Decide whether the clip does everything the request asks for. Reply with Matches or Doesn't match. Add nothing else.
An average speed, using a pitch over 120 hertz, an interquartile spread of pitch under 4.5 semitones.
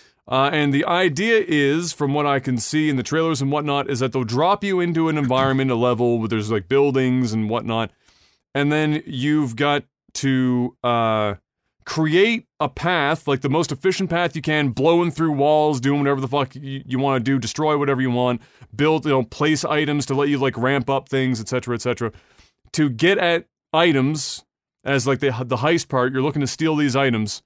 Doesn't match